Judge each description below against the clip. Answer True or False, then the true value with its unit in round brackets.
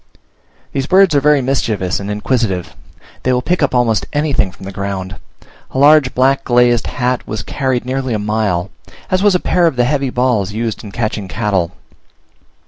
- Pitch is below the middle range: True (120 Hz)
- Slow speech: False (180 wpm)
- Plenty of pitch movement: False (4.8 semitones)